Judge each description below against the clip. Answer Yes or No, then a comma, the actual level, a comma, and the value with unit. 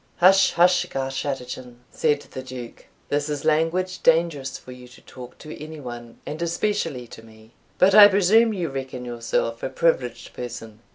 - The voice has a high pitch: No, medium, 140 Hz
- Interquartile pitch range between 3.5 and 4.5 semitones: No, wide, 5.5 semitones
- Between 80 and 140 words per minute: No, average, 165 wpm